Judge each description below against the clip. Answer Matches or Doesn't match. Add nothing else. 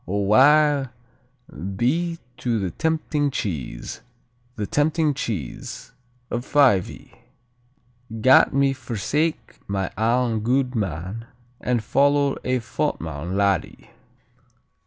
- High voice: Doesn't match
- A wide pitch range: Matches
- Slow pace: Matches